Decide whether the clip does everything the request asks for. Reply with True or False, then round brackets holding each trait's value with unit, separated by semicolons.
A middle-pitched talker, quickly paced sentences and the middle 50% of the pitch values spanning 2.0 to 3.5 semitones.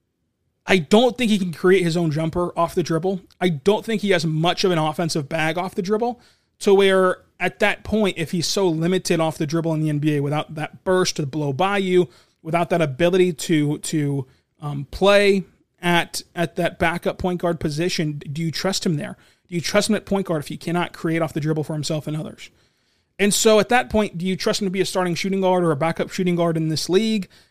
True (175 Hz; 235 wpm; 2.9 semitones)